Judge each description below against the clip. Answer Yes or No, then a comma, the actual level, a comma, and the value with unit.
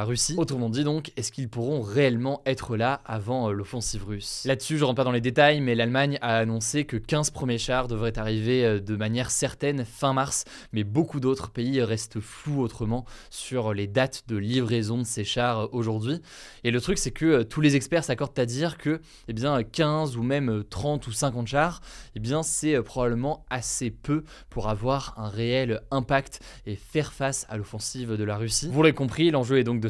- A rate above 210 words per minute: No, average, 195 wpm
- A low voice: Yes, low, 125 Hz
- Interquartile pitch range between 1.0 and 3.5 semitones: No, average, 3.9 semitones